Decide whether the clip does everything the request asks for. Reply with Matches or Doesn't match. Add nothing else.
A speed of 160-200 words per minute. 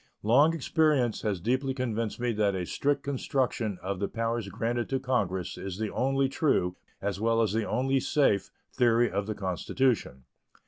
Matches